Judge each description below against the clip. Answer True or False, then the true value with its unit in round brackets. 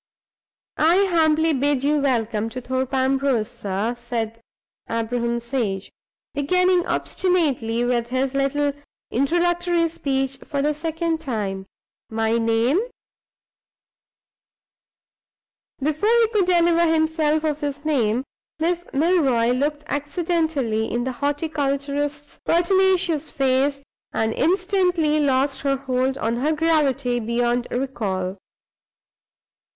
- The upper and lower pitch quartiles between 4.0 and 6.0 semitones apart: True (4.9 semitones)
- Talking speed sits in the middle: False (105 wpm)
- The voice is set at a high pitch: True (280 Hz)